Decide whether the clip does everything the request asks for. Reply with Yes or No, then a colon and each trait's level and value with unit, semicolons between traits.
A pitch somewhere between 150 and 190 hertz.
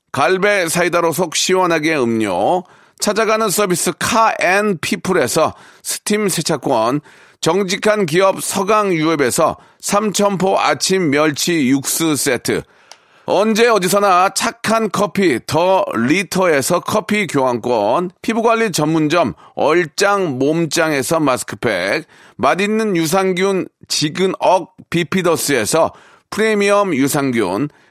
Yes: medium, 185 Hz